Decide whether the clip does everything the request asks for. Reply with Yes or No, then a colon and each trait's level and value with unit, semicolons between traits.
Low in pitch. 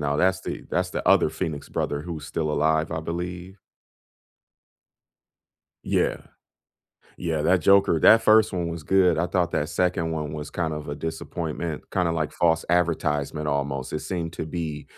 Yes: very low, 80 Hz